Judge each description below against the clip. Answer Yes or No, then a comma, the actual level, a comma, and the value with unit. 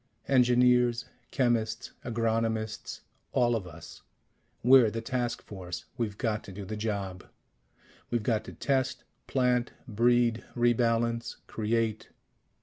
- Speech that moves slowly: Yes, slow, 120 wpm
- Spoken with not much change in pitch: Yes, narrow, 2.0 semitones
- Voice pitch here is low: Yes, low, 115 Hz